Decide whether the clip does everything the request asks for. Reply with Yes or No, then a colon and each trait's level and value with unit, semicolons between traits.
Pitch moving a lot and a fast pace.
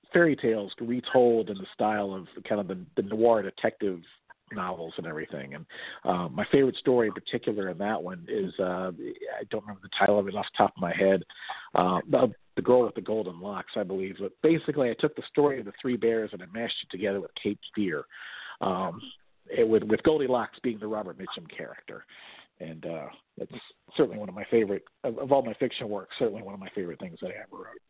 No: average, 3.8 semitones; fast, 220 wpm